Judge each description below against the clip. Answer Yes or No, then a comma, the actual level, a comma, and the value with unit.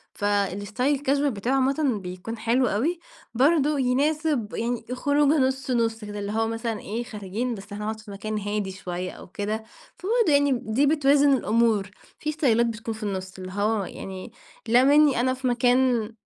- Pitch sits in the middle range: No, high, 230 Hz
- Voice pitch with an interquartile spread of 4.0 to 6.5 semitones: Yes, average, 4.6 semitones